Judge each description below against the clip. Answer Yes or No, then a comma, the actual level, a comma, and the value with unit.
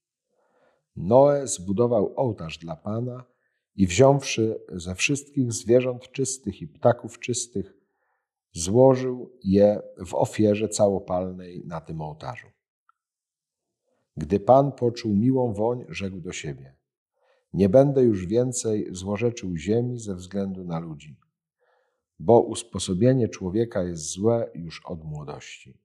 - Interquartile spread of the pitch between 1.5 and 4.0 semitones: No, average, 5.1 semitones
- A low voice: Yes, low, 105 Hz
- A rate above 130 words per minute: No, slow, 110 wpm